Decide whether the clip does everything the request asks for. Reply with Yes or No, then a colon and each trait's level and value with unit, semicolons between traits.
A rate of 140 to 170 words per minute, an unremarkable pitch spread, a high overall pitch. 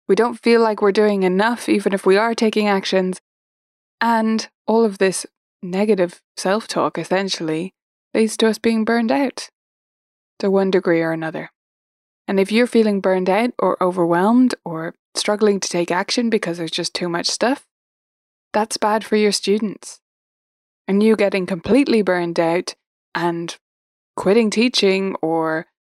Yes: average, 155 wpm; average, 3.5 semitones; high, 200 Hz